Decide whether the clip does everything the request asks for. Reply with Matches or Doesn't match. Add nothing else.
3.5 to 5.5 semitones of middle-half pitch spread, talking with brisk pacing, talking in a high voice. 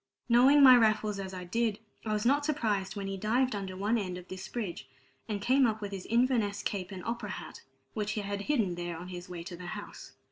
Matches